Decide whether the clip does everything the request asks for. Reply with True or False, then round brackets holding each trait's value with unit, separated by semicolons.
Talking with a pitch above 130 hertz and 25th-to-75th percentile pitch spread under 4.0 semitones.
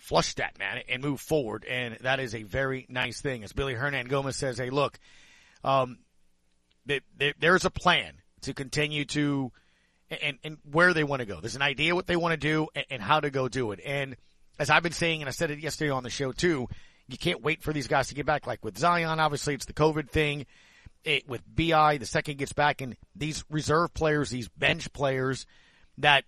True (140 Hz; 3.1 semitones)